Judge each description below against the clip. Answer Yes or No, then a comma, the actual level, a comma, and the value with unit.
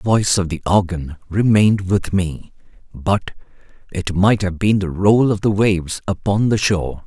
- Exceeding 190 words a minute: No, average, 180 wpm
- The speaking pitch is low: Yes, very low, 95 Hz